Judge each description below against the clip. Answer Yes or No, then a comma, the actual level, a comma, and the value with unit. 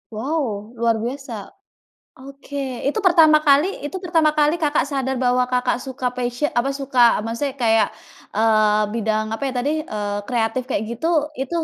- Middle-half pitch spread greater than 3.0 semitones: Yes, average, 4.0 semitones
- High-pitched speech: Yes, very high, 255 Hz